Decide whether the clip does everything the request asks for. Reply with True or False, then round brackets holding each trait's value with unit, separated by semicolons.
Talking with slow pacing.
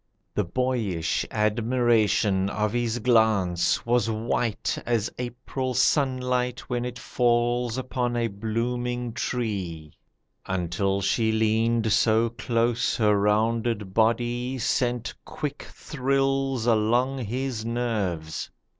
True (100 wpm)